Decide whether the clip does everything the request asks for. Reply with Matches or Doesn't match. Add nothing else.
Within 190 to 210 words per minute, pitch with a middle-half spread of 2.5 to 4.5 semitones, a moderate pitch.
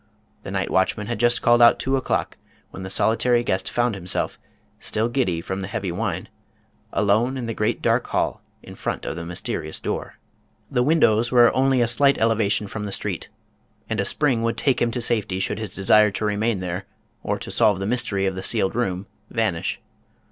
Doesn't match